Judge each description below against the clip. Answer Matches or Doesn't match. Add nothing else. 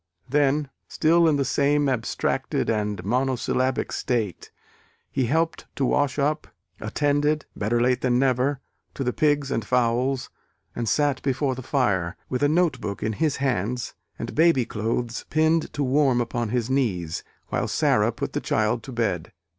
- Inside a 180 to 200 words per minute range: Doesn't match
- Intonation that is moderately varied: Matches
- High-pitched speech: Doesn't match